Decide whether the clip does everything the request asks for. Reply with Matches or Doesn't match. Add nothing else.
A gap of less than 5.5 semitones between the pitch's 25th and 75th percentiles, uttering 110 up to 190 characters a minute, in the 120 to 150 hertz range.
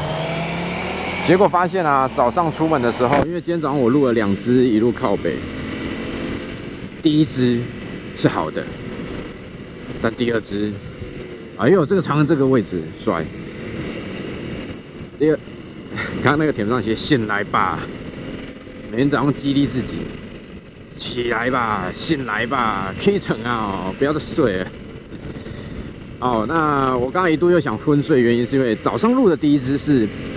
Doesn't match